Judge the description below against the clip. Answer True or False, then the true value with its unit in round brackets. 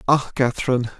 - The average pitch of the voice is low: True (130 Hz)